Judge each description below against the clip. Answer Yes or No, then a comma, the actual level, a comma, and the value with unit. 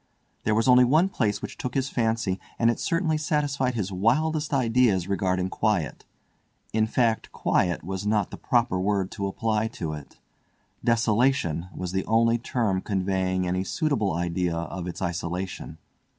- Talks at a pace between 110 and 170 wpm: Yes, average, 150 wpm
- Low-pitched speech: Yes, low, 105 Hz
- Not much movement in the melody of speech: No, average, 4.8 semitones